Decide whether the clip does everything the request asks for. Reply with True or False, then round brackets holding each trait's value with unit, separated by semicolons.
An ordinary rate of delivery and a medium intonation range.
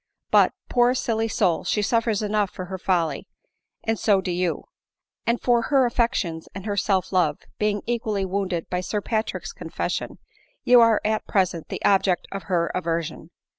True (165 wpm; 3.6 semitones)